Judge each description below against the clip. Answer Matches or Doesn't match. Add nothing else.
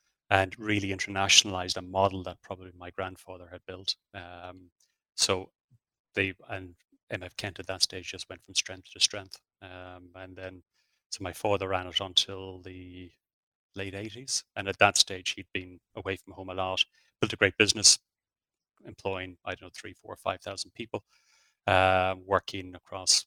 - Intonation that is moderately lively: Doesn't match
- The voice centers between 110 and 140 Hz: Doesn't match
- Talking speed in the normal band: Matches